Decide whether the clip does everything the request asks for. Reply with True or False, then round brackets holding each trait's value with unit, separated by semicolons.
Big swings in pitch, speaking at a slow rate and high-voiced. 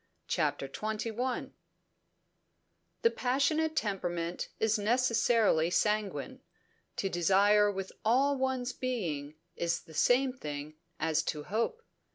True (6.6 semitones; 105 wpm; 215 Hz)